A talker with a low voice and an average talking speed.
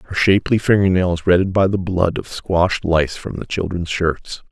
Yes: very low, 90 Hz; average, 185 wpm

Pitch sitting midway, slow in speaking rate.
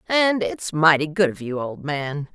No: medium, 160 Hz; fast, 205 wpm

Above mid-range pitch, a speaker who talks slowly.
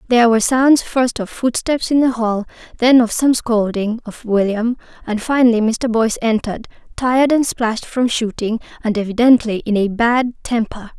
No: high, 230 Hz; average, 170 wpm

